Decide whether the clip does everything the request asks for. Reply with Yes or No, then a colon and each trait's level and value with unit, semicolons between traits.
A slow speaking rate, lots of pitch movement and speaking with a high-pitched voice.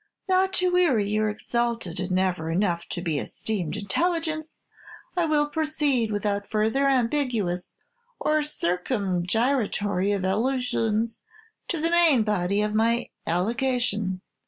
Yes: slow, 115 wpm; wide, 6.6 semitones; high, 220 Hz